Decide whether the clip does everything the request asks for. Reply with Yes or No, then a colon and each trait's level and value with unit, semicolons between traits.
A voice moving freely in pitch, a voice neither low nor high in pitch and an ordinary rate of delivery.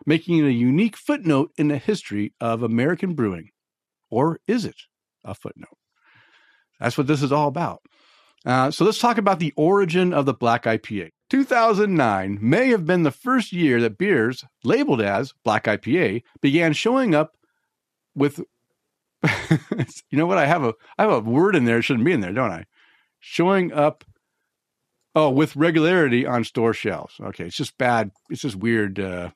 Yes: wide, 6.9 semitones; medium, 145 Hz; average, 180 wpm